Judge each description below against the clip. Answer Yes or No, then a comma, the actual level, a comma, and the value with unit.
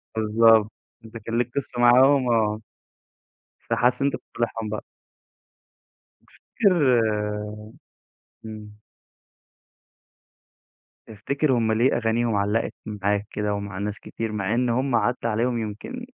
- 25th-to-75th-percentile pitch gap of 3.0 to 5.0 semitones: No, narrow, 2.6 semitones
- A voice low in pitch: Yes, low, 115 Hz